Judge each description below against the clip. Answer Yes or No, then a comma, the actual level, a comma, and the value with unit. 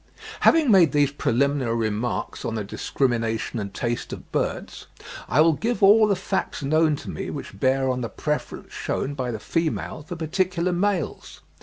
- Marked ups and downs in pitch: Yes, wide, 6.6 semitones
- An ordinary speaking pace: Yes, average, 170 wpm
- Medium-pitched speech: Yes, medium, 145 Hz